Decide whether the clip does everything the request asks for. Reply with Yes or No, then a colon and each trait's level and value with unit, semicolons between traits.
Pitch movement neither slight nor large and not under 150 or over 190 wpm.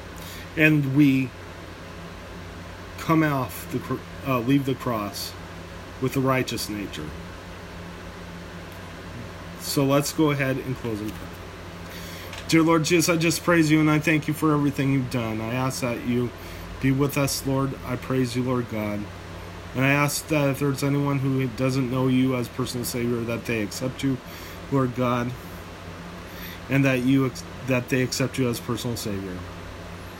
No: wide, 7.2 semitones; average, 160 wpm